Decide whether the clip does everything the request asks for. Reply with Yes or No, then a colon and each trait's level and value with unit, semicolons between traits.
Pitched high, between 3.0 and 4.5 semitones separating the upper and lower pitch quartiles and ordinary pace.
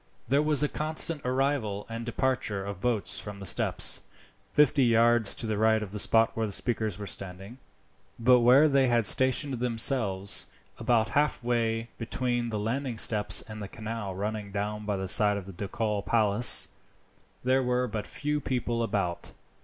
No: low, 115 Hz; average, 3.4 semitones; average, 170 wpm